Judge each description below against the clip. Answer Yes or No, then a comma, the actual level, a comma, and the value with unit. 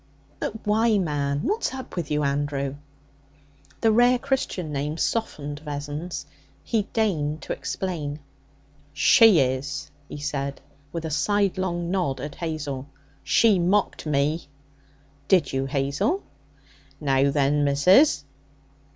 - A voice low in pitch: No, medium, 150 Hz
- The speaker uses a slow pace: Yes, slow, 115 wpm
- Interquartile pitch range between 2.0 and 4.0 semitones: No, average, 5.3 semitones